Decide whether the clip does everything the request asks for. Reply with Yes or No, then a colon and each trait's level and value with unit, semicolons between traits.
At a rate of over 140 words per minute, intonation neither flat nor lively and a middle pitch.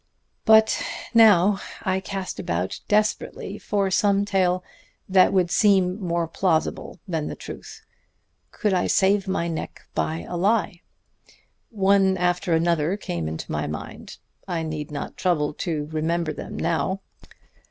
No: slow, 135 wpm; average, 3.5 semitones; medium, 180 Hz